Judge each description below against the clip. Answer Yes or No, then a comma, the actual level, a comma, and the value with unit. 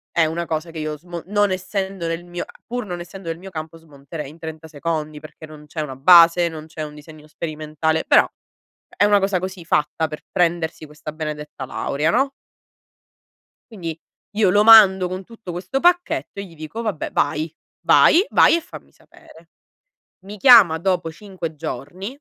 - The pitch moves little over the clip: No, average, 3.6 semitones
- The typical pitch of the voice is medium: Yes, medium, 165 Hz